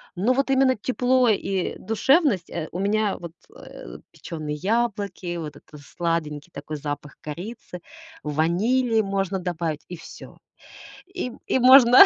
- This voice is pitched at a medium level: No, high, 195 Hz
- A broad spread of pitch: Yes, wide, 6.5 semitones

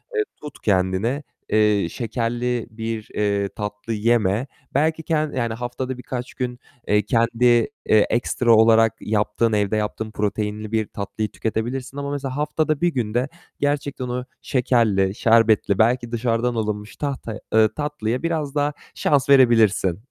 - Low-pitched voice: Yes, low, 115 Hz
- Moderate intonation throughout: Yes, average, 3.5 semitones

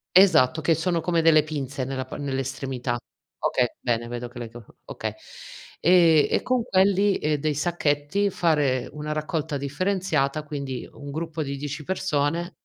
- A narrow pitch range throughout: No, average, 3.7 semitones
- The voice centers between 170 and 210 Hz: No, medium, 150 Hz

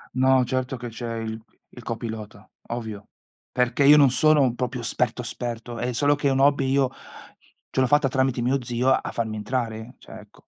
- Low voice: Yes, low, 125 Hz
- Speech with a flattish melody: Yes, narrow, 2.3 semitones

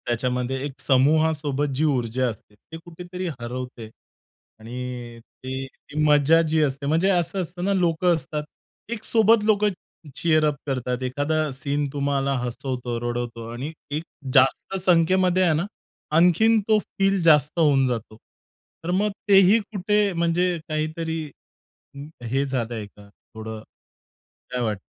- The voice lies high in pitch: No, medium, 145 Hz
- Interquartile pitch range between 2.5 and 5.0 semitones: No, wide, 5.6 semitones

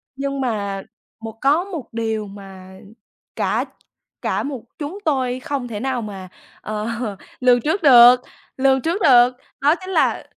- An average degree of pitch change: Yes, average, 4.3 semitones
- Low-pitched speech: No, very high, 250 Hz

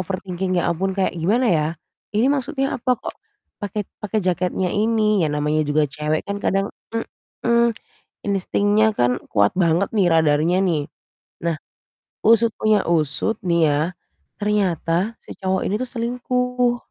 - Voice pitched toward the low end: No, high, 190 Hz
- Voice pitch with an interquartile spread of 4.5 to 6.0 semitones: Yes, average, 4.9 semitones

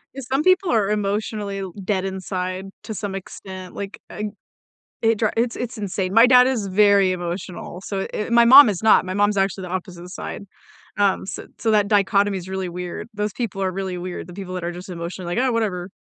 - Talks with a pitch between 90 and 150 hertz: No, high, 195 Hz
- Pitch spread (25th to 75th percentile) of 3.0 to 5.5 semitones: No, narrow, 2.6 semitones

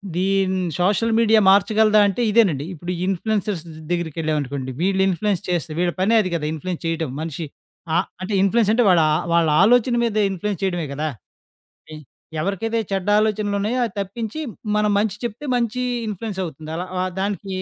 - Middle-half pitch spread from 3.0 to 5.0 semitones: Yes, average, 3.7 semitones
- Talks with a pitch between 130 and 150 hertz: No, high, 195 Hz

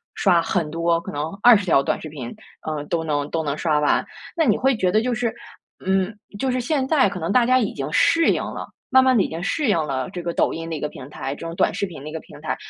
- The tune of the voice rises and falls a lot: Yes, wide, 6.9 semitones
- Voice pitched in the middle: Yes, medium, 170 Hz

